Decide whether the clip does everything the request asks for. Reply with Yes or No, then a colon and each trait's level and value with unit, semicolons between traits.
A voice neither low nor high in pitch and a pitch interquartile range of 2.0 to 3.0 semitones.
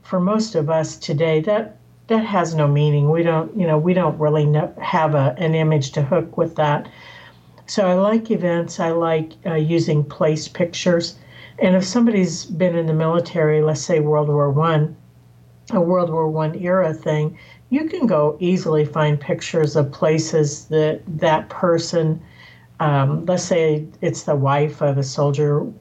Yes: medium, 160 Hz; narrow, 2.5 semitones